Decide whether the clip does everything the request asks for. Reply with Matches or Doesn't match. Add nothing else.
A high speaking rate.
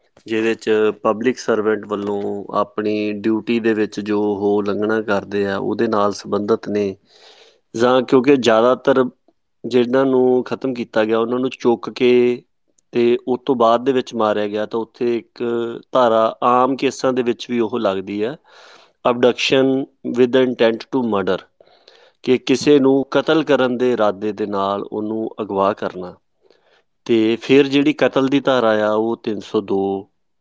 Doesn't match